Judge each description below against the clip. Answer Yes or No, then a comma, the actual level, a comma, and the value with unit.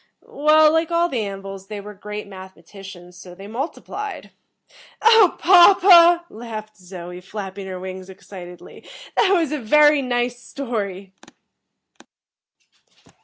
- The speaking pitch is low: No, high, 215 Hz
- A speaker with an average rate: No, slow, 120 wpm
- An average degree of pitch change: No, wide, 8.2 semitones